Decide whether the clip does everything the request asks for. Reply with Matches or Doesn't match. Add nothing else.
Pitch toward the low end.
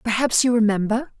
Doesn't match